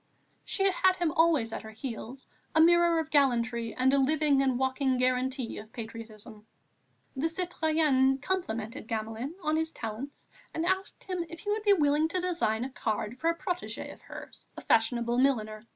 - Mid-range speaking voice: No, very high, 270 Hz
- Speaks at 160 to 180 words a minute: Yes, average, 175 wpm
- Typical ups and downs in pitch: No, wide, 5.9 semitones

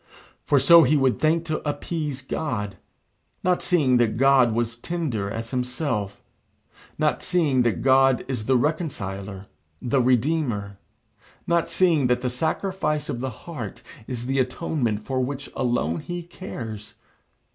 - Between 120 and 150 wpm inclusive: Yes, average, 145 wpm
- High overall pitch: No, low, 130 Hz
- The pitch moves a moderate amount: Yes, average, 4.8 semitones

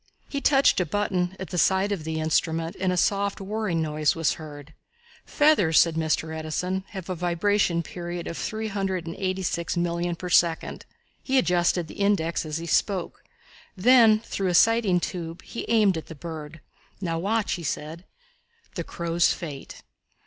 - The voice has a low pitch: No, medium, 175 Hz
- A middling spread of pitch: Yes, average, 3.3 semitones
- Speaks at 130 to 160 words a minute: No, average, 170 wpm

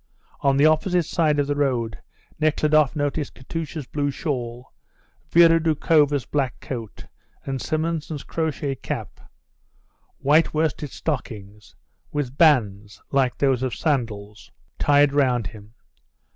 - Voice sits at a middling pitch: Yes, medium, 145 Hz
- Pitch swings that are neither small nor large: Yes, average, 3.9 semitones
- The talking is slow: Yes, slow, 115 wpm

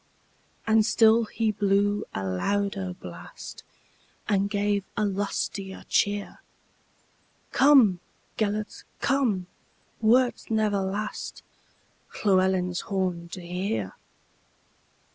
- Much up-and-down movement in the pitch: No, narrow, 2.4 semitones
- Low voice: No, high, 200 Hz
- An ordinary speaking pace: No, slow, 75 wpm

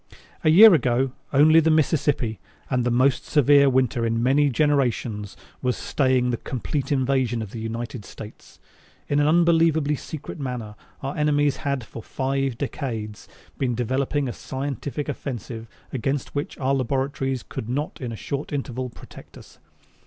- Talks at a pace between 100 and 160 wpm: Yes, average, 150 wpm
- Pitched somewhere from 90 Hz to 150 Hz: Yes, low, 135 Hz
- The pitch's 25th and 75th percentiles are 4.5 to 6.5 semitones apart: No, average, 3.1 semitones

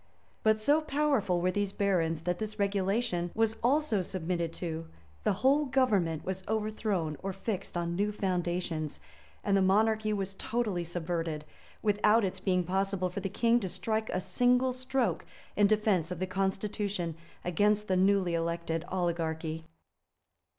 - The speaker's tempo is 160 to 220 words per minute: No, average, 150 wpm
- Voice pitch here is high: Yes, high, 195 Hz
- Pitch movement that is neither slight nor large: Yes, average, 3.6 semitones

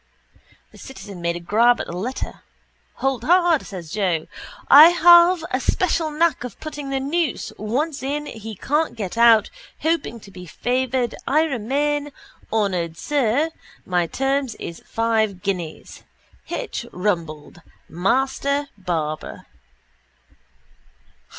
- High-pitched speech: Yes, high, 245 Hz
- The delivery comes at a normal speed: No, slow, 125 wpm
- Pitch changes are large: Yes, wide, 7.2 semitones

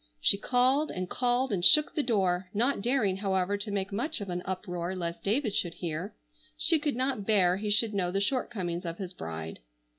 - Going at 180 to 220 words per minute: Yes, average, 200 wpm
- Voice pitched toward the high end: Yes, high, 200 Hz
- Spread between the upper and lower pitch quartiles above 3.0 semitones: Yes, average, 5.2 semitones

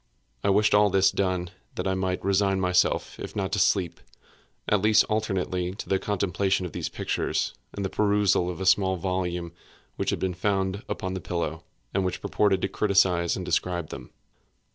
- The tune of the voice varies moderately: No, narrow, 1.7 semitones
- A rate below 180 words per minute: No, average, 185 wpm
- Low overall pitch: Yes, very low, 95 Hz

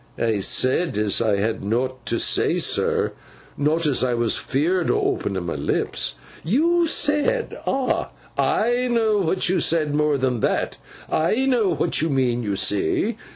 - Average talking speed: Yes, average, 160 wpm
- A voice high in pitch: No, medium, 150 Hz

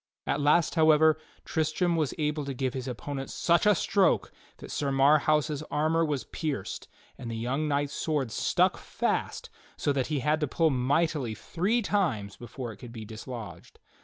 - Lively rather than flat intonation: No, average, 3.6 semitones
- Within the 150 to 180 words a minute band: Yes, average, 170 wpm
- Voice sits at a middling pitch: Yes, medium, 145 Hz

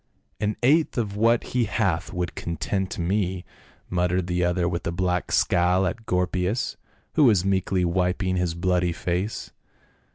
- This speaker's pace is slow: No, average, 150 wpm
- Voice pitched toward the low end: Yes, very low, 90 Hz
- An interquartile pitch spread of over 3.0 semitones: No, narrow, 2.5 semitones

